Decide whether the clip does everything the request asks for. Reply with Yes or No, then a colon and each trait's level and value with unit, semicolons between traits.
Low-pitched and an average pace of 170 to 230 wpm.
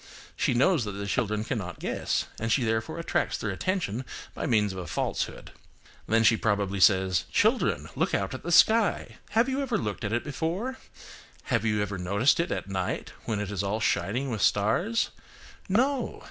Yes: low, 110 Hz; average, 180 wpm